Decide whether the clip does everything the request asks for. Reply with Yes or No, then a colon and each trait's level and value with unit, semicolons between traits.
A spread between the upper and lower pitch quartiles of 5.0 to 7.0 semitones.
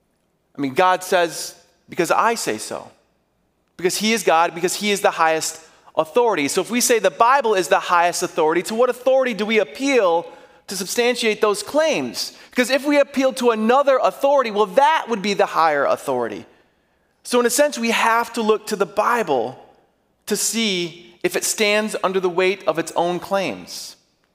Yes: average, 5.3 semitones